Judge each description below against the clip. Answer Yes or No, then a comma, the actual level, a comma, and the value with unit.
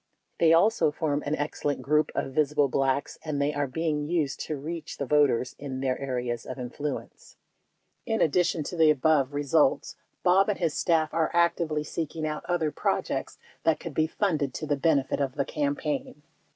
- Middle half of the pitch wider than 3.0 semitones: No, narrow, 2.5 semitones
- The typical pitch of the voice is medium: Yes, medium, 150 Hz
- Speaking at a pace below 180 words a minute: No, average, 185 wpm